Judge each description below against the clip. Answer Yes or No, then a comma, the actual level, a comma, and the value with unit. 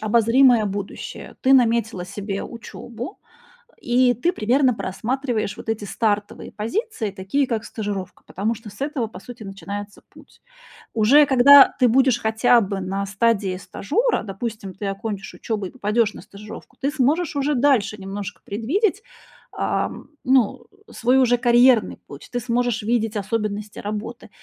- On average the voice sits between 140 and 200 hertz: No, high, 225 Hz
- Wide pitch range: No, average, 3.6 semitones